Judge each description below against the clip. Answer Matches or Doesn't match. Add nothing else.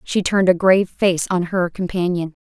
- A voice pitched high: Doesn't match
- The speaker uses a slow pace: Doesn't match